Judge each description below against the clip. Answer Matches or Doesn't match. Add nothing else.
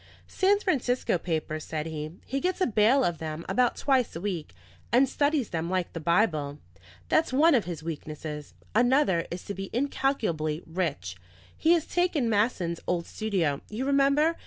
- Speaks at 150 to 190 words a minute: Matches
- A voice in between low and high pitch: Doesn't match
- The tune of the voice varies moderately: Doesn't match